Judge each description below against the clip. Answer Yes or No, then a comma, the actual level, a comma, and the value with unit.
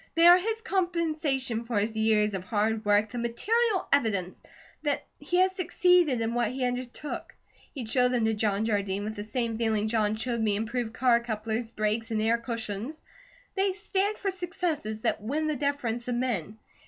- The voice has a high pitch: Yes, high, 235 Hz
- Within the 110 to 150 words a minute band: No, average, 180 wpm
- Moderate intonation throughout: No, wide, 5.9 semitones